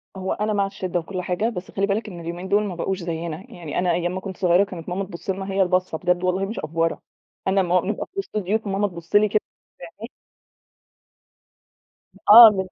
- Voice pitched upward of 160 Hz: Yes, high, 190 Hz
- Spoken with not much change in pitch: Yes, narrow, 2.3 semitones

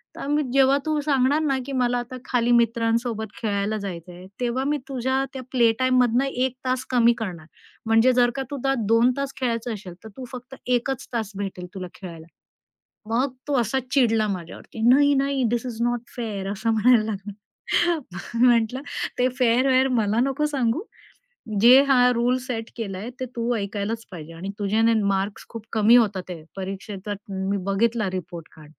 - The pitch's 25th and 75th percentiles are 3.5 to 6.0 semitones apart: Yes, average, 3.8 semitones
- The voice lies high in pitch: Yes, high, 235 Hz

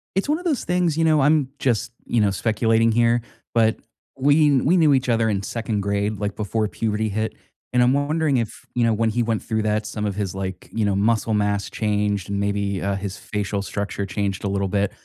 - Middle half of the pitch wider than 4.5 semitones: No, average, 3.4 semitones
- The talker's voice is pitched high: No, low, 110 Hz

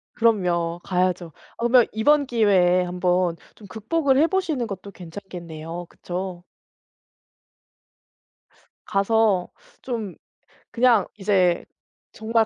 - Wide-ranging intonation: No, average, 4.5 semitones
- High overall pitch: Yes, high, 195 Hz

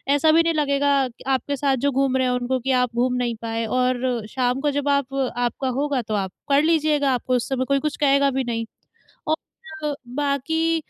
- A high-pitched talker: Yes, very high, 270 Hz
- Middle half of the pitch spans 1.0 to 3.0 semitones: Yes, narrow, 2.4 semitones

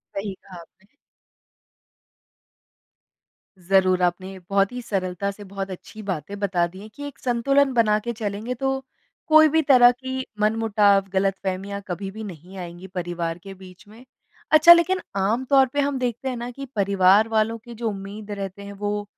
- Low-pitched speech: No, high, 205 Hz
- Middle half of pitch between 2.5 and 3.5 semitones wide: No, average, 4.1 semitones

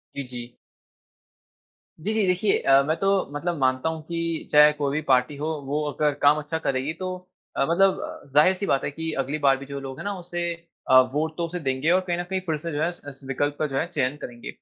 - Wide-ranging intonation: No, average, 3.6 semitones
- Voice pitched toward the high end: No, medium, 150 Hz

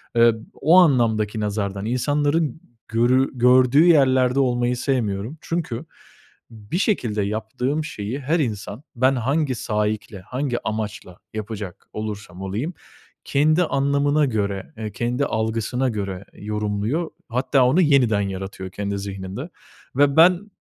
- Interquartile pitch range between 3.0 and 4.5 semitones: No, average, 5.1 semitones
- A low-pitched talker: Yes, low, 120 Hz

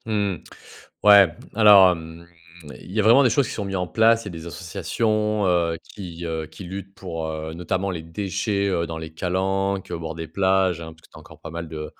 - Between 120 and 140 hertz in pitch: No, very low, 90 Hz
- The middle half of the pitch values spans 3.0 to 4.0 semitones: Yes, average, 3.3 semitones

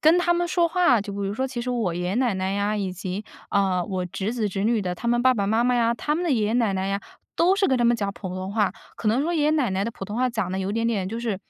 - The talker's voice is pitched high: Yes, high, 220 Hz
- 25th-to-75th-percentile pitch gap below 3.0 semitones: No, average, 4.3 semitones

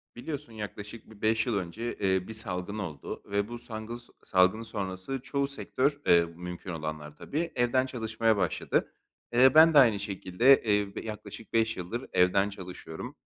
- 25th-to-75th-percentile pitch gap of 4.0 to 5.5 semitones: Yes, average, 4.3 semitones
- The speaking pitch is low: Yes, low, 105 Hz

